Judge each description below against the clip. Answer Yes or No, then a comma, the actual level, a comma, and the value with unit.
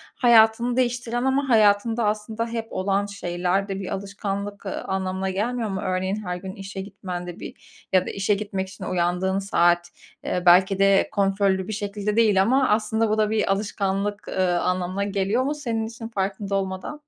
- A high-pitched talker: Yes, high, 200 Hz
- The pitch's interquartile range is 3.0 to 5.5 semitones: No, narrow, 2.6 semitones